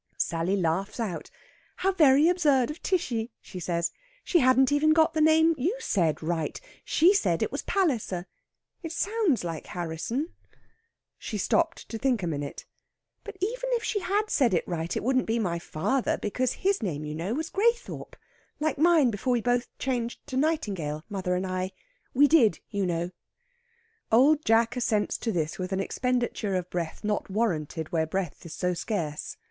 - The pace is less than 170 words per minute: No, average, 175 wpm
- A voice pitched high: Yes, high, 230 Hz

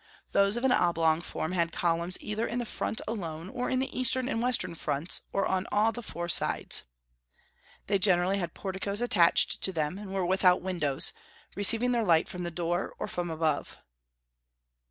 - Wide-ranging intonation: No, average, 4.0 semitones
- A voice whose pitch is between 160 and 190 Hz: Yes, medium, 185 Hz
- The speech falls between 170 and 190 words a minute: Yes, average, 180 wpm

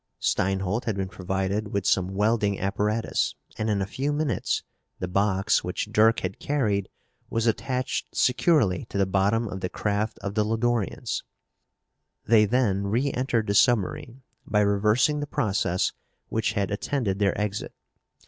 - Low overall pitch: Yes, low, 105 Hz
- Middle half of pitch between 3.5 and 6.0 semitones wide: No, average, 3.0 semitones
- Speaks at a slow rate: No, average, 150 wpm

